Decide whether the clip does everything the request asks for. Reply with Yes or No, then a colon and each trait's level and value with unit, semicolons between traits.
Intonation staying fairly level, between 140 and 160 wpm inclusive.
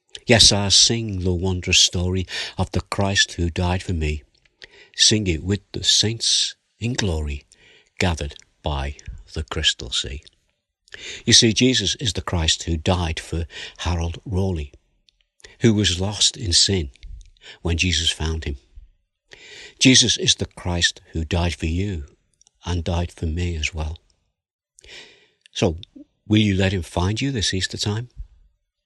No: average, 3.6 semitones; average, 145 wpm